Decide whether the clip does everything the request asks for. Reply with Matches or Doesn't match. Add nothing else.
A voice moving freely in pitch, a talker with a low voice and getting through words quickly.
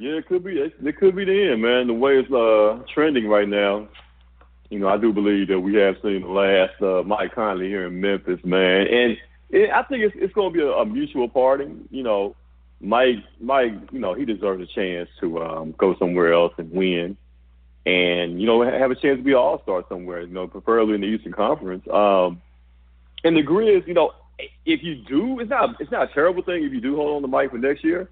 Matches